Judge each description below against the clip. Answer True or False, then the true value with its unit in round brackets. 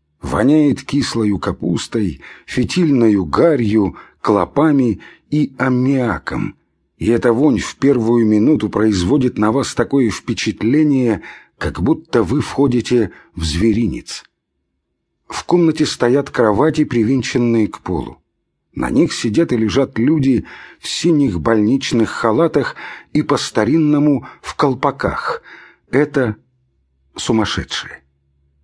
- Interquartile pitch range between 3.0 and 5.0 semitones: False (5.5 semitones)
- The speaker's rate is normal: False (100 wpm)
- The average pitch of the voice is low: True (120 Hz)